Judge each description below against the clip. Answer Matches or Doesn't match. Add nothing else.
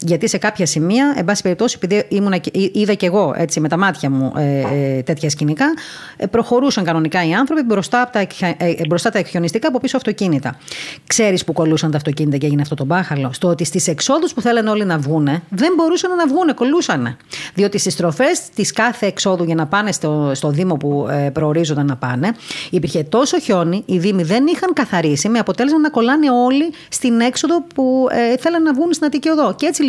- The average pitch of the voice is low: Doesn't match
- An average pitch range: Doesn't match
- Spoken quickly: Matches